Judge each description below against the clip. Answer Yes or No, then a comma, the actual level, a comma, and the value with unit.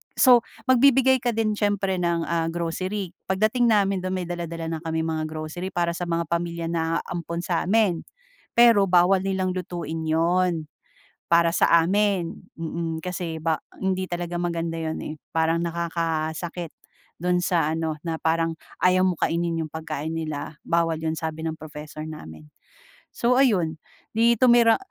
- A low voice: No, medium, 170 Hz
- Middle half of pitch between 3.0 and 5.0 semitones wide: No, narrow, 2.5 semitones